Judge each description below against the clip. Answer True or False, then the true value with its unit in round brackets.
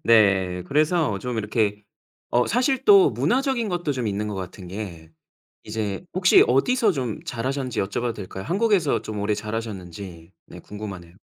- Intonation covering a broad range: True (7.7 semitones)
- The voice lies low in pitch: True (110 Hz)